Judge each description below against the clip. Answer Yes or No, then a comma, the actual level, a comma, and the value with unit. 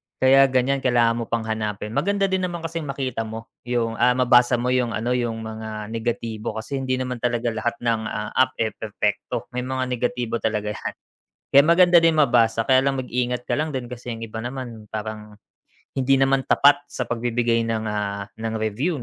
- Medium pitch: No, low, 120 Hz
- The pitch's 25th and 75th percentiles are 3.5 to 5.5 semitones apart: No, average, 2.8 semitones